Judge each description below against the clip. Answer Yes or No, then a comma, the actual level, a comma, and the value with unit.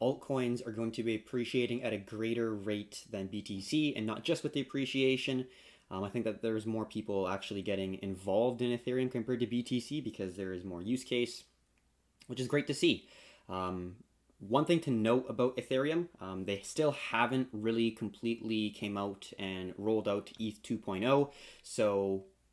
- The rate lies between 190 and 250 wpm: No, average, 175 wpm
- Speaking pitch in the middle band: No, low, 115 Hz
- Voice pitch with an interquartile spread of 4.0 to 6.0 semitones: Yes, average, 4.3 semitones